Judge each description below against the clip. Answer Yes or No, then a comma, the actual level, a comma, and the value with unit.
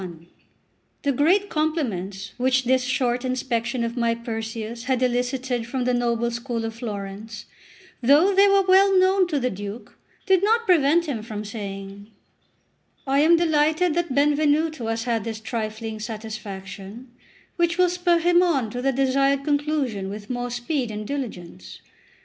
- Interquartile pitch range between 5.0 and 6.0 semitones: Yes, wide, 5.5 semitones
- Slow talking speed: No, average, 155 wpm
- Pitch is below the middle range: No, very high, 250 Hz